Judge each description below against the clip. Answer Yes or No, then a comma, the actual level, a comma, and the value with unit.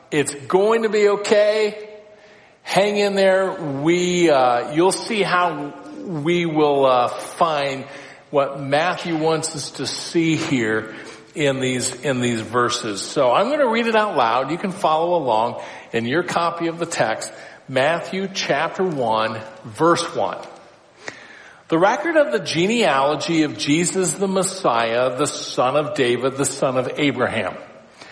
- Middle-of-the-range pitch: Yes, medium, 155 Hz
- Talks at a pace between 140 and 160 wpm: Yes, average, 145 wpm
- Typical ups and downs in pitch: No, wide, 5.8 semitones